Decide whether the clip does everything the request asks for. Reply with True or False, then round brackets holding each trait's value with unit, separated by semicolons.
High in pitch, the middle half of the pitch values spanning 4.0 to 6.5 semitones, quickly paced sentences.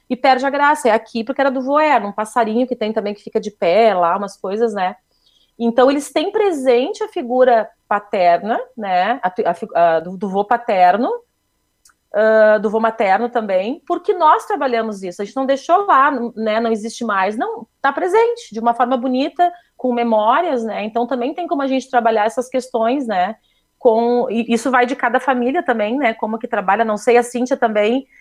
False (240 Hz; 3.6 semitones; 200 wpm)